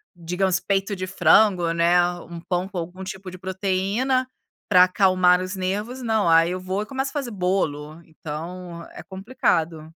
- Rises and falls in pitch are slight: Yes, narrow, 2.3 semitones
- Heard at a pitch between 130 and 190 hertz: Yes, medium, 185 Hz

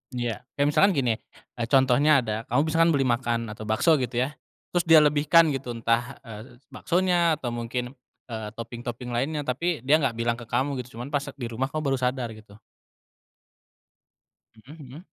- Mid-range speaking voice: No, low, 125 Hz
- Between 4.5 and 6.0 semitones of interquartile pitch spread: No, average, 3.8 semitones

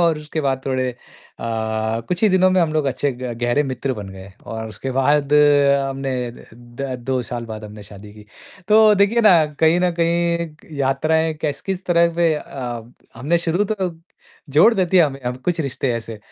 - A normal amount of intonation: No, wide, 5.8 semitones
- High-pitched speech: No, medium, 140 Hz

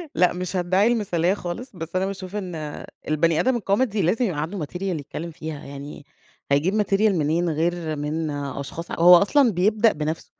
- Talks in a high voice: No, medium, 175 Hz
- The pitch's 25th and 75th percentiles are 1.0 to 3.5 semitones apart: No, average, 4.1 semitones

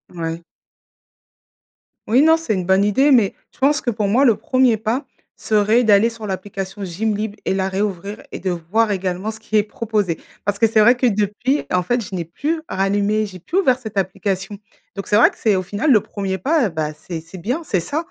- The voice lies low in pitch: No, high, 210 Hz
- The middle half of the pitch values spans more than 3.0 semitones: Yes, average, 3.4 semitones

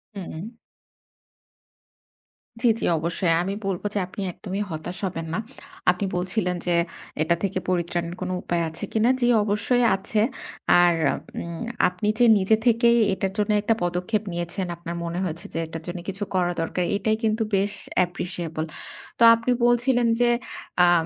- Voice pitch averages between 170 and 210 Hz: Yes, medium, 185 Hz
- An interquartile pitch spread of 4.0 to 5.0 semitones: No, average, 3.5 semitones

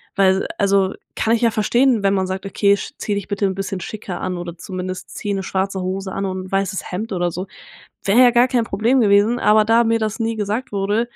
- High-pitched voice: Yes, high, 200 Hz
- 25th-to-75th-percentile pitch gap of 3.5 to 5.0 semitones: No, average, 2.9 semitones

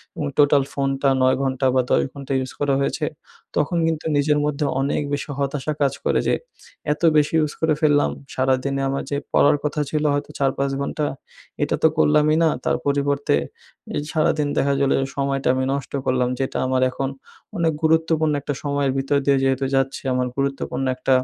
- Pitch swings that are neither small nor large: No, narrow, 1.7 semitones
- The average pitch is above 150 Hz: No, medium, 140 Hz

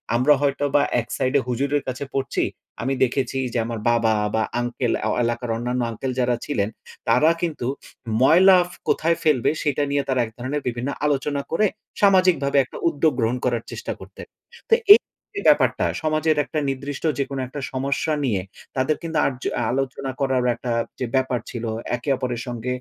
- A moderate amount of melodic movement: Yes, average, 3.0 semitones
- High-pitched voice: No, low, 135 Hz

